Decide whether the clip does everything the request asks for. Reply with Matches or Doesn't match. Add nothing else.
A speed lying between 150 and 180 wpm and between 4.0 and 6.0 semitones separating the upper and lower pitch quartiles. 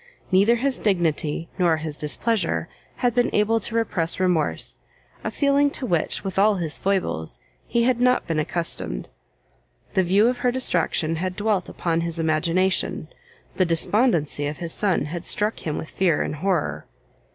Matches